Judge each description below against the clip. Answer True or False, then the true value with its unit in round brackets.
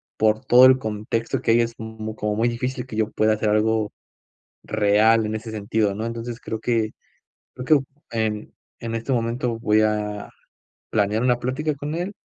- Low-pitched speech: True (110 Hz)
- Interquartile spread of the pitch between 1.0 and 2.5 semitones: True (2.0 semitones)